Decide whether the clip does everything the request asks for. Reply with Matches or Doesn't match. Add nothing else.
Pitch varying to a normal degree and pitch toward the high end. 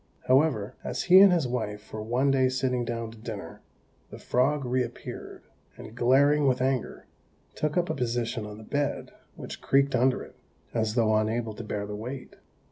Doesn't match